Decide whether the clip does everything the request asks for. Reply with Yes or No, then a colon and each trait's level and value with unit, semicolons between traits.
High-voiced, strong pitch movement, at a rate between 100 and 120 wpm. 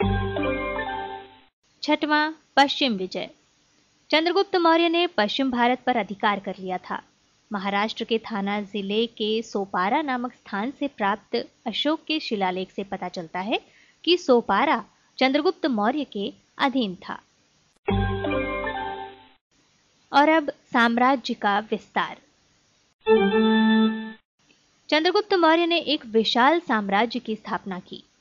Yes: high, 220 Hz; wide, 6.2 semitones; slow, 110 wpm